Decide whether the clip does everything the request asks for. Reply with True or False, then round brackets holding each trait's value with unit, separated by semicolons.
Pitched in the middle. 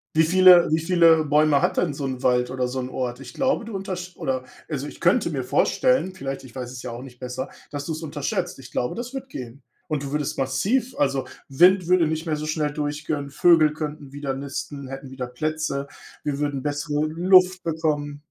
True (150 Hz)